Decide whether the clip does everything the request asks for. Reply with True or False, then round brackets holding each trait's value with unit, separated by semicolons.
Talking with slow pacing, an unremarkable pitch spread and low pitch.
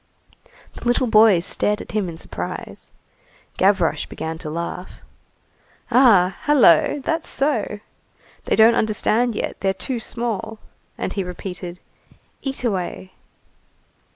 False (120 wpm; 4.8 semitones; 210 Hz)